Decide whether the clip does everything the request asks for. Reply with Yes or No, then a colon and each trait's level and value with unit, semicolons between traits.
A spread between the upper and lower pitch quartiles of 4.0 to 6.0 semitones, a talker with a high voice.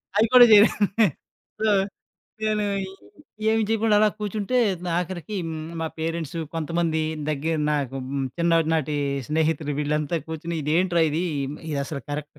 No: average, 4.7 semitones; medium, 165 Hz